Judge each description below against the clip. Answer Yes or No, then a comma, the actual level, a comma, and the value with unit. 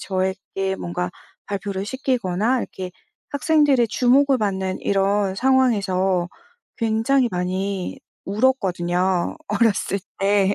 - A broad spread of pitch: No, average, 4.4 semitones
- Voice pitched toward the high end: Yes, high, 200 Hz